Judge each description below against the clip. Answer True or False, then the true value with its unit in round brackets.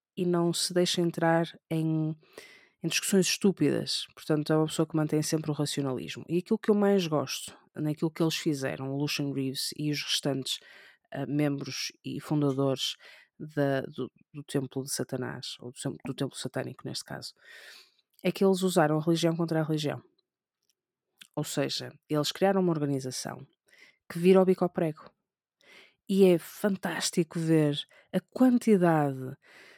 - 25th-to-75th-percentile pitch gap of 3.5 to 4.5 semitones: True (4.0 semitones)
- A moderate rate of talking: True (155 wpm)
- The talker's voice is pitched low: False (155 Hz)